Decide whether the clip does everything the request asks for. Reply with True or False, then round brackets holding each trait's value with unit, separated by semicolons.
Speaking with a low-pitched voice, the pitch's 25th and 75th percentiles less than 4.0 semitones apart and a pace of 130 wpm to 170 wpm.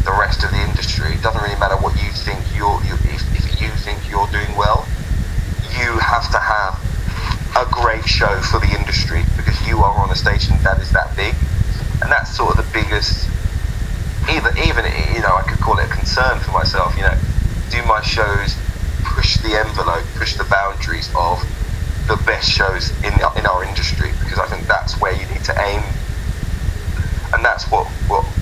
False (95 Hz; 2.9 semitones; 190 wpm)